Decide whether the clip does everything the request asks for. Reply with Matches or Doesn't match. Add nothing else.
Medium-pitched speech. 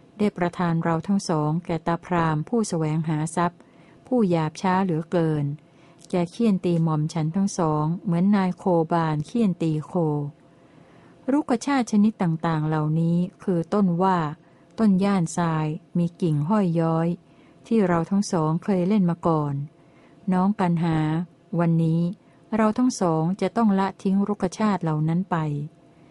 Matches